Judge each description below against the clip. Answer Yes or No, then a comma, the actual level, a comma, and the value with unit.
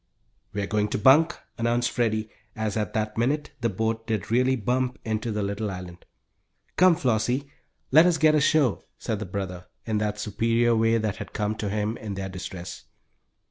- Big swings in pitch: No, average, 2.9 semitones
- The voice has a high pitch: No, low, 110 Hz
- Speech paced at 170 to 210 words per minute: Yes, average, 180 wpm